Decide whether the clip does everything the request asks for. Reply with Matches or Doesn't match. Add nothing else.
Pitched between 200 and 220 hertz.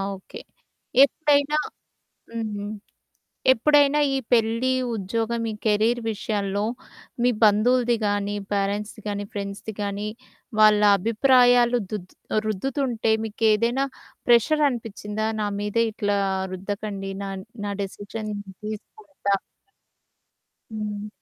Matches